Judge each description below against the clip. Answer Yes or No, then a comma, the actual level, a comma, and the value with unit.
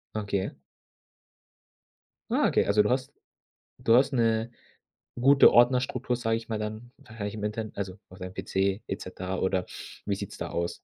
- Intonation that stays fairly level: No, average, 3.6 semitones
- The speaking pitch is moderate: No, low, 110 Hz